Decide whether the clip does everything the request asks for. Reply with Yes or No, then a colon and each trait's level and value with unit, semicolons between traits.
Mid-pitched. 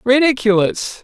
No: high, 230 Hz